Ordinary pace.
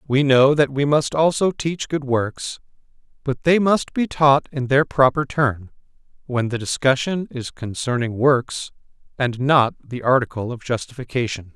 Yes: average, 155 wpm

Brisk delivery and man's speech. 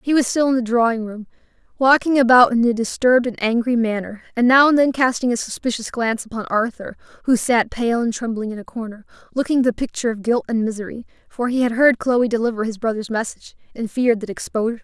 No: fast, 220 wpm; female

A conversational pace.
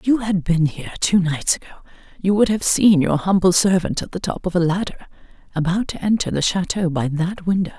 No: fast, 225 wpm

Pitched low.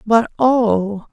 No: high, 220 Hz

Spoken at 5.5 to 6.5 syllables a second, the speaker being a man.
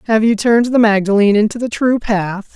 Yes: 5.9 syllables/s; male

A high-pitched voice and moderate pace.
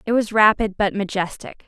Yes: high, 205 Hz; average, 180 wpm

